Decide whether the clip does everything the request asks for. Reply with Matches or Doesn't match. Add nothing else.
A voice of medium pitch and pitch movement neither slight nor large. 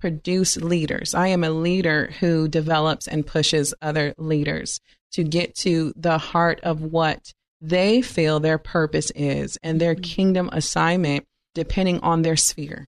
Doesn't match